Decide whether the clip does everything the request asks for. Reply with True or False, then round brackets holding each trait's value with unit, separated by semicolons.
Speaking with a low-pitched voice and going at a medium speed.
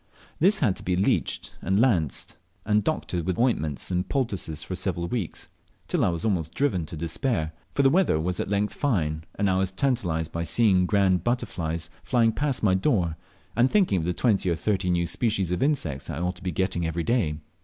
False (95 Hz; 210 wpm)